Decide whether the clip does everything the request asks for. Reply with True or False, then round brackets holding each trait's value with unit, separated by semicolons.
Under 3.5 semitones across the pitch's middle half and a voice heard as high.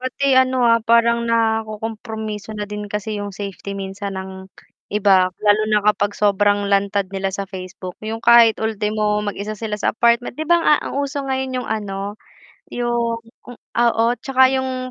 True (2.6 semitones; 215 Hz)